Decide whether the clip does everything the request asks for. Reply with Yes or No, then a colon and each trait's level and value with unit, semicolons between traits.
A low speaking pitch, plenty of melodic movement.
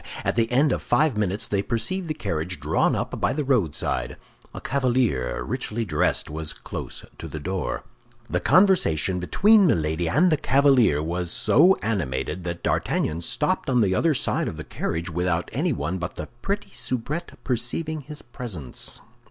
Yes: low, 110 Hz; wide, 9.0 semitones